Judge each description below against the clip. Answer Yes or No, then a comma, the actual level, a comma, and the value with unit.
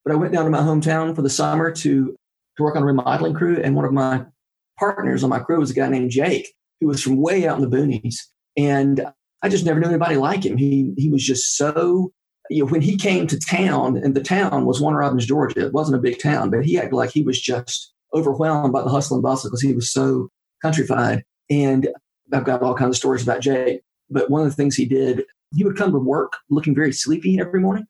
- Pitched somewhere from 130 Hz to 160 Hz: Yes, medium, 140 Hz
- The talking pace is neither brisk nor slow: No, fast, 245 wpm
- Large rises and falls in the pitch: No, average, 3.3 semitones